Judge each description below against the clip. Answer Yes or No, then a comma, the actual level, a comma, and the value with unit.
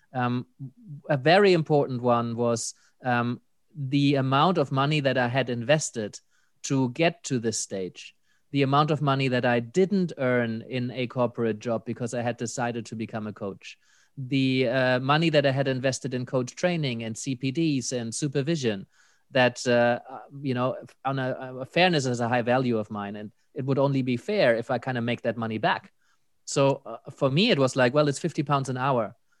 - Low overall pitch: Yes, low, 130 Hz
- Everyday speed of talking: Yes, average, 195 wpm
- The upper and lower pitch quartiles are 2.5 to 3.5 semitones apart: Yes, average, 2.9 semitones